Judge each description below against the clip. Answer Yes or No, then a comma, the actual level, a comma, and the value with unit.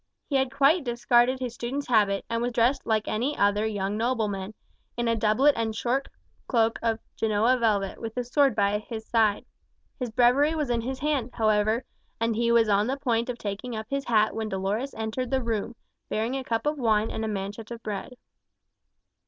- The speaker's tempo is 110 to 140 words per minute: No, average, 195 wpm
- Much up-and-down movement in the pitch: No, average, 2.8 semitones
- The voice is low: No, high, 230 Hz